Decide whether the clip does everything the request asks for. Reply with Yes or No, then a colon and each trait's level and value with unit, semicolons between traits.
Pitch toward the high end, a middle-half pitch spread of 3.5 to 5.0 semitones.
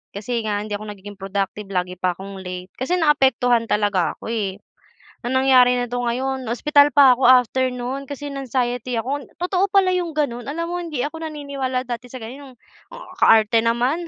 Yes: very high, 250 Hz; average, 4.6 semitones